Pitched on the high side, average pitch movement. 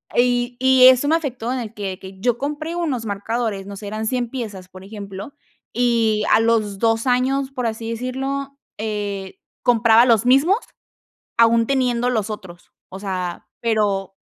Yes: high, 230 Hz; average, 3.6 semitones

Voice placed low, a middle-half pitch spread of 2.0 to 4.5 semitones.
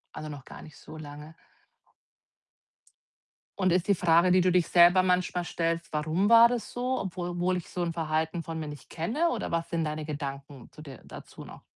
No: medium, 170 Hz; average, 2.9 semitones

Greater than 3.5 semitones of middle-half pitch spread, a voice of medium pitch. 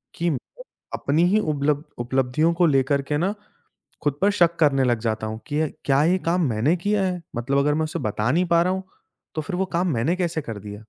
Yes: average, 4.6 semitones; medium, 150 Hz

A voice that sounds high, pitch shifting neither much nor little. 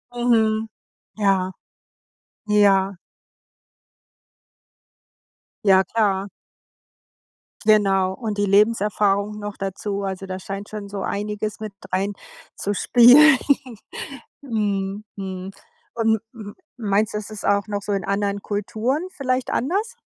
No: high, 205 Hz; narrow, 1.8 semitones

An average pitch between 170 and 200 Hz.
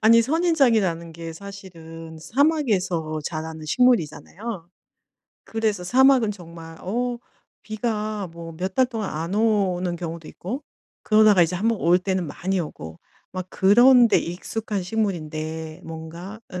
Yes: high, 190 Hz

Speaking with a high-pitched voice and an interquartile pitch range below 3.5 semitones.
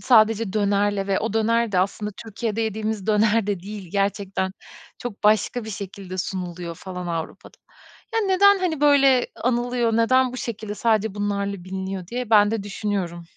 Yes: high, 210 Hz; average, 2.8 semitones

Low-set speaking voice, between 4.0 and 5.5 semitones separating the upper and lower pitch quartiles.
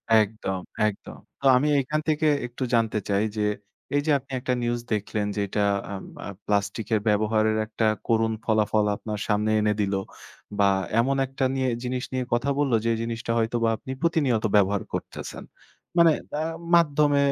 No: low, 115 Hz; average, 3.6 semitones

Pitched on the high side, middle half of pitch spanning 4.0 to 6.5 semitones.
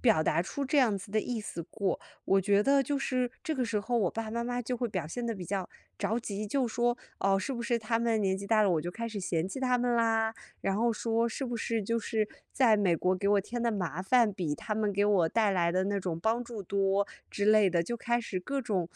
No: high, 215 Hz; average, 3.5 semitones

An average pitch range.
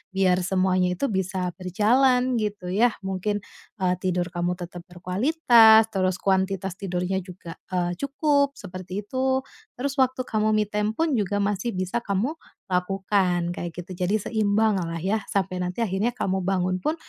Yes: average, 3.2 semitones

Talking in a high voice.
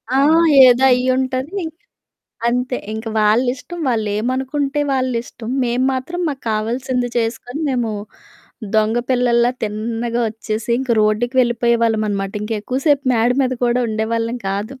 Yes: high, 240 Hz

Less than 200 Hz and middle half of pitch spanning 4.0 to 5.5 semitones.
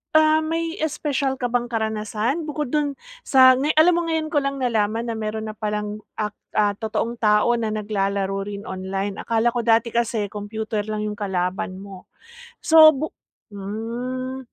No: high, 225 Hz; average, 4.5 semitones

